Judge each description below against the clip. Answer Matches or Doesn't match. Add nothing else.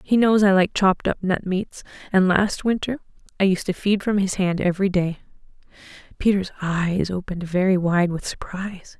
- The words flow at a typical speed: Matches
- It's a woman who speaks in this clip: Matches